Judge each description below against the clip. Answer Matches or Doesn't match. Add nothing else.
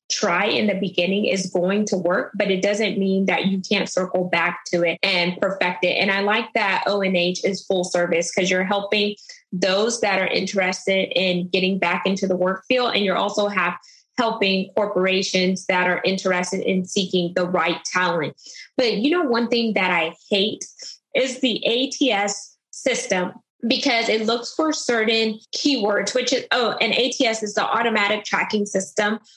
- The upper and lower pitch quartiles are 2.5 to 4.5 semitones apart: Matches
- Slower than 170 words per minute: Doesn't match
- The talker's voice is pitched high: Matches